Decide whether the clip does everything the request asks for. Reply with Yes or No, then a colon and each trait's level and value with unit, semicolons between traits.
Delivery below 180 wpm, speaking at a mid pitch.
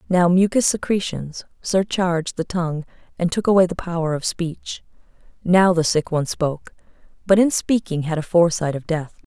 Yes: average, 170 wpm; medium, 175 Hz